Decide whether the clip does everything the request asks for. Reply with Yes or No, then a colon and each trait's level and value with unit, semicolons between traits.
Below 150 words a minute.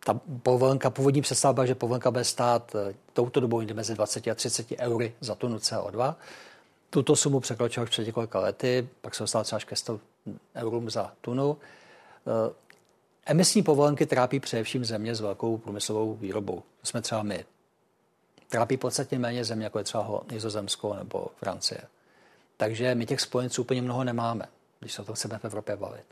No: average, 165 wpm